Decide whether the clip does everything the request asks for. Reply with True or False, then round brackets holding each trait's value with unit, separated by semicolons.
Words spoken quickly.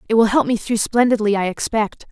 True (225 wpm)